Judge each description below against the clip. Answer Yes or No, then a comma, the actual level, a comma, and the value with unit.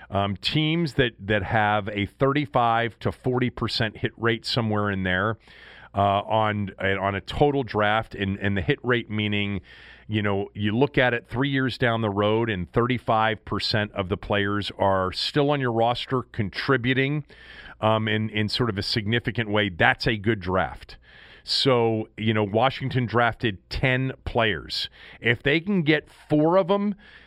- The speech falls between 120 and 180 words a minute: Yes, average, 170 wpm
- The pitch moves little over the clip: No, average, 3.6 semitones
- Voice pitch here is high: No, low, 115 Hz